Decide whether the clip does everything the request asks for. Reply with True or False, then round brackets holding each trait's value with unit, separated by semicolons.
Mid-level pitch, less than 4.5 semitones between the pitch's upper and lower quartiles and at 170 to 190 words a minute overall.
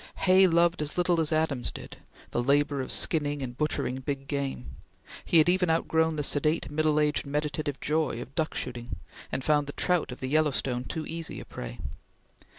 True (150 Hz; 2.9 semitones; 185 wpm)